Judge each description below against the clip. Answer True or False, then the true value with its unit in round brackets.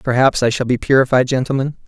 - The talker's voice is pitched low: True (130 Hz)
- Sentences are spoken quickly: False (190 wpm)